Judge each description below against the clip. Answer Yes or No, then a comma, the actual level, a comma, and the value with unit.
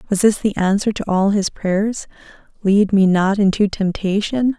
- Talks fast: No, average, 170 wpm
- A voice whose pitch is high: Yes, high, 200 Hz